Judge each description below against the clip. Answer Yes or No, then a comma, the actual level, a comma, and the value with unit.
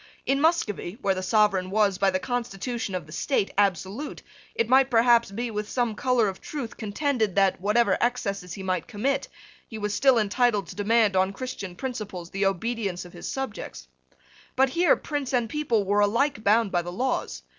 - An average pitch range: Yes, average, 4.2 semitones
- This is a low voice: No, high, 215 Hz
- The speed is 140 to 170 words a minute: No, average, 185 wpm